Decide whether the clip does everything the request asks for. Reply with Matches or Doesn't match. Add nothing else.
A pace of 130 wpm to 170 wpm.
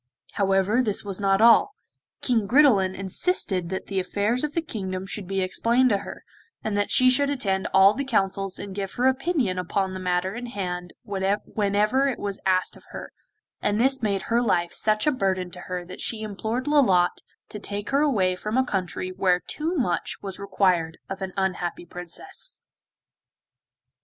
Doesn't match